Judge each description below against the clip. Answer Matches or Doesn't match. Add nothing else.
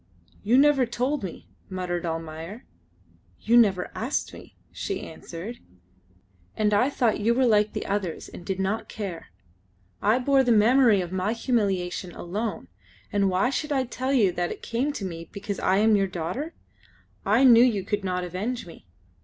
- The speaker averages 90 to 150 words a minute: Doesn't match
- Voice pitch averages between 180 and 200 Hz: Doesn't match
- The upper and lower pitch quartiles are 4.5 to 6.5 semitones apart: Matches